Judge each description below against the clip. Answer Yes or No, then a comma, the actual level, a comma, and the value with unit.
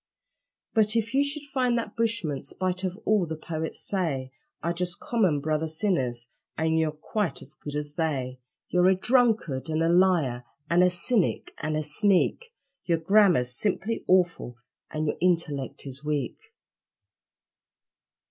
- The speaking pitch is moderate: Yes, medium, 170 Hz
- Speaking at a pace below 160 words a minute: Yes, average, 150 wpm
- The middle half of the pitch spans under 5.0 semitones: No, average, 5.3 semitones